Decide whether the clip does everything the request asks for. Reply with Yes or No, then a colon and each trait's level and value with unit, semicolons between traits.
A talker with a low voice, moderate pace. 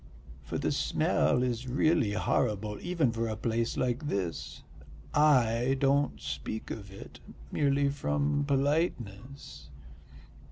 No: low, 120 Hz; slow, 115 wpm